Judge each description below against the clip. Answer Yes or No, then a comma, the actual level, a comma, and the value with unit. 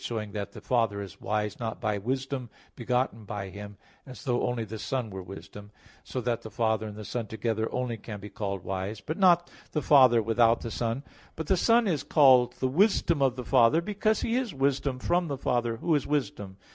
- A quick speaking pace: Yes, fast, 220 wpm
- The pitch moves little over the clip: No, average, 4.4 semitones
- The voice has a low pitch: Yes, low, 120 Hz